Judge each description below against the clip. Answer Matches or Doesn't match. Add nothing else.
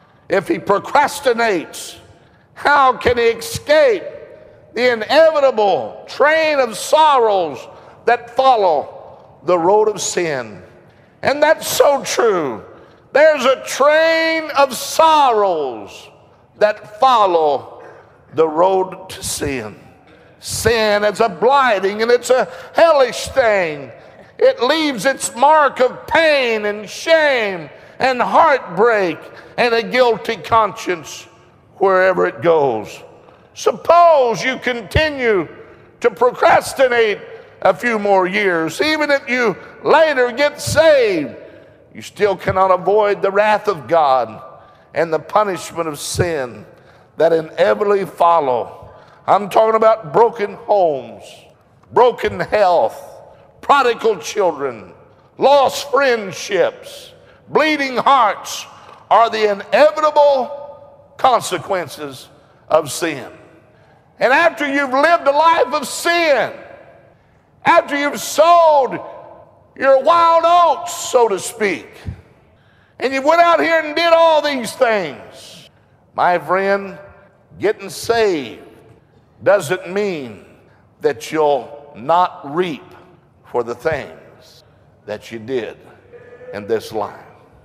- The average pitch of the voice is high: Matches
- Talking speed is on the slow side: Matches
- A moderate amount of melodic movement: Doesn't match